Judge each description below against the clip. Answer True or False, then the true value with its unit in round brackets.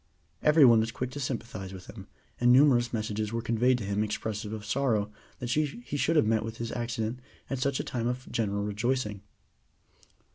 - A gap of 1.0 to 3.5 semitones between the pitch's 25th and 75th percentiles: True (3.2 semitones)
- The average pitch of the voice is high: False (115 Hz)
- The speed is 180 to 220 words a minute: True (190 wpm)